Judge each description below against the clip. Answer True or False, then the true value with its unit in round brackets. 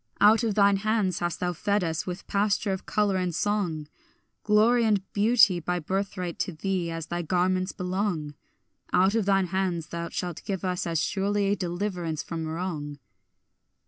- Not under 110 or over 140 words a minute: False (165 wpm)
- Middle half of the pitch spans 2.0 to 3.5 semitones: True (2.9 semitones)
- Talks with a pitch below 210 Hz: True (185 Hz)